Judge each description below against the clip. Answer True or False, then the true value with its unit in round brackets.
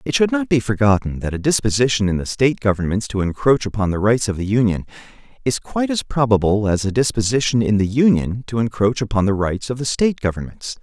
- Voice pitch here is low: True (115 Hz)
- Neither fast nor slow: False (215 wpm)